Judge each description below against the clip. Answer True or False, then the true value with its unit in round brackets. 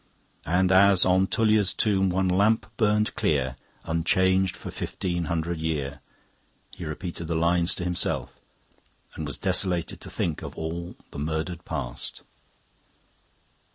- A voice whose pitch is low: True (90 Hz)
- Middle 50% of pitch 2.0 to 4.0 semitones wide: True (2.8 semitones)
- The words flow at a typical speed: False (130 wpm)